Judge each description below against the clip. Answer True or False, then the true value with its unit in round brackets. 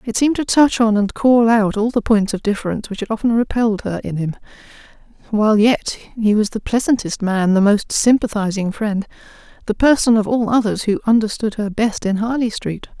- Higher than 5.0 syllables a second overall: True (5.5 syllables/s)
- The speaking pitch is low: False (220 Hz)